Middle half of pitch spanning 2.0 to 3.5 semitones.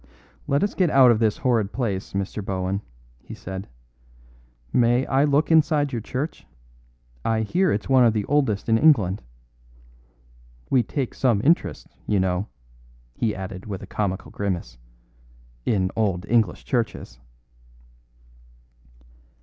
No: wide, 5.5 semitones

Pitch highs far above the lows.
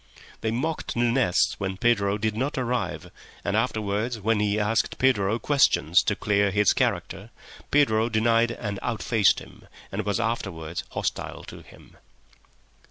No: average, 2.8 semitones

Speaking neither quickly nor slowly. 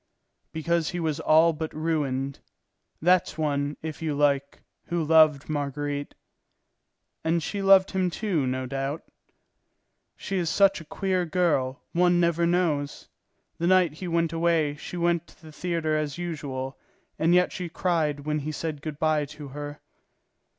Yes: average, 155 wpm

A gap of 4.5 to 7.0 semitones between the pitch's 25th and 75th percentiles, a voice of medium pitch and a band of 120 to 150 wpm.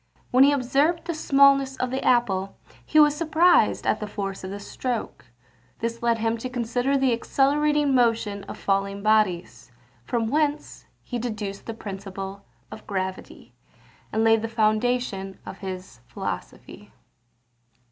No: average, 5.2 semitones; high, 230 Hz; average, 145 wpm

